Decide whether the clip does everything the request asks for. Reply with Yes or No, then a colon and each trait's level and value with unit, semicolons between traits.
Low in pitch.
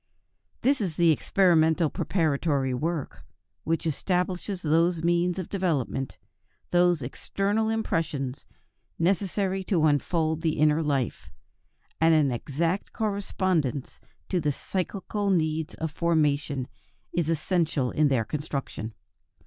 No: medium, 165 Hz